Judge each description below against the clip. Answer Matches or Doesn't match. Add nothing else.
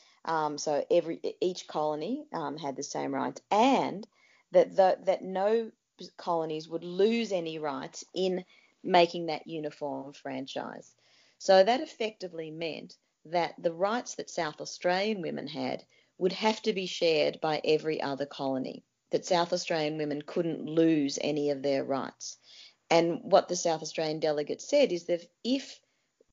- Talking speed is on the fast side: Doesn't match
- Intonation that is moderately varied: Matches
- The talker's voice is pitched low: Doesn't match